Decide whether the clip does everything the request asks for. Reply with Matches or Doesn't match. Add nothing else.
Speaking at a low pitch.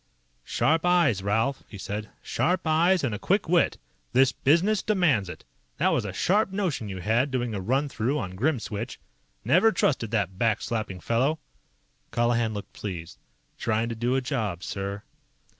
Matches